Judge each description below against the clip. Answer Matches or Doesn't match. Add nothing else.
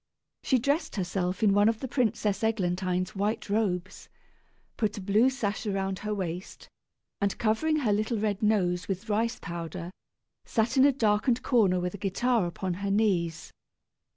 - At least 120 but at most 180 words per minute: Matches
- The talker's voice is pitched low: Doesn't match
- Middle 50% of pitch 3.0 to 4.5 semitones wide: Matches